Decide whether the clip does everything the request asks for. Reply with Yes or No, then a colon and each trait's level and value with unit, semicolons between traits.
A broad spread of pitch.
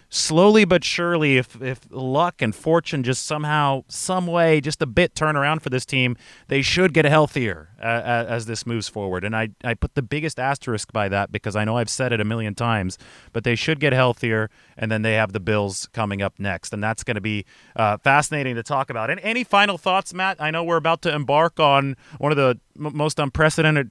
Yes: wide, 5.8 semitones